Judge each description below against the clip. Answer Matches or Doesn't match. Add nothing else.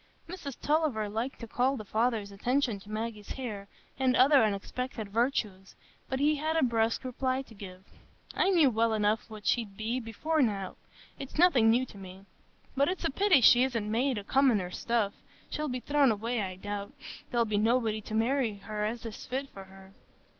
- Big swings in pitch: Doesn't match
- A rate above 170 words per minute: Matches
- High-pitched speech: Matches